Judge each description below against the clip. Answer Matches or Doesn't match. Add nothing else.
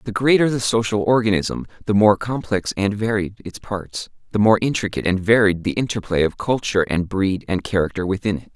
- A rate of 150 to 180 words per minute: Doesn't match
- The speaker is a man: Matches